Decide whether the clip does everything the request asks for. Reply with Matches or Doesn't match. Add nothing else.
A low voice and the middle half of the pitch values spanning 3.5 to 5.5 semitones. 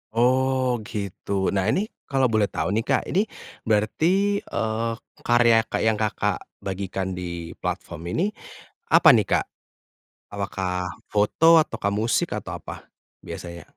Matches